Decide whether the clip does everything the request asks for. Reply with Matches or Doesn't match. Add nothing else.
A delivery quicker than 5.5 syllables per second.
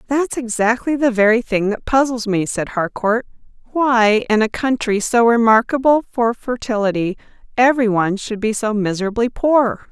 Doesn't match